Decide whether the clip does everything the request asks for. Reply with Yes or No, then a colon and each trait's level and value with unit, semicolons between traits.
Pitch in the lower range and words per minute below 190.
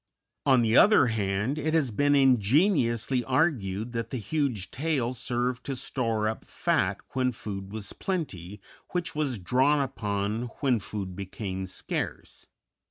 Yes: low, 120 Hz; average, 140 wpm